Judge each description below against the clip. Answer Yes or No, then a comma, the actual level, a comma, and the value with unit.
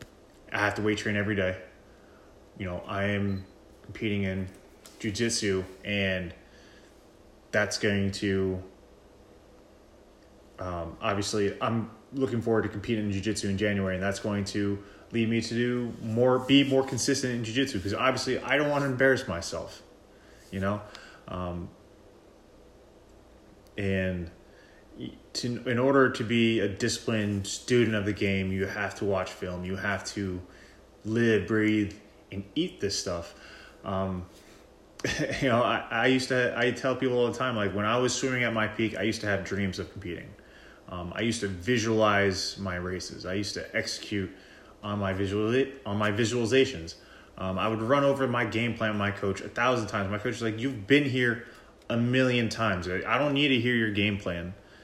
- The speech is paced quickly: No, average, 170 wpm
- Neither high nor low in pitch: No, low, 105 Hz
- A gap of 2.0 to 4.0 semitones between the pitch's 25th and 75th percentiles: Yes, average, 3.2 semitones